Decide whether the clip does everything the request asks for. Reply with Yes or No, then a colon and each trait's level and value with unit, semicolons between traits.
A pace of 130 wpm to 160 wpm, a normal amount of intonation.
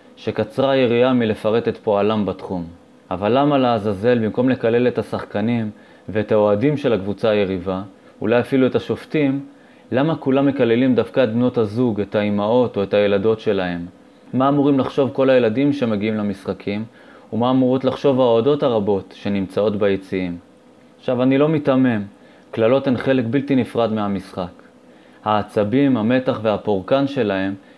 Yes: average, 135 wpm; average, 4.4 semitones